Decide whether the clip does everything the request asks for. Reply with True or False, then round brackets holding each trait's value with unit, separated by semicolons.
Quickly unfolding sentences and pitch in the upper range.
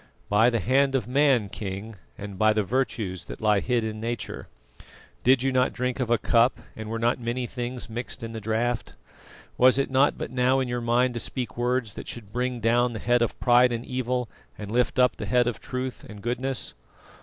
False (210 wpm; 120 Hz)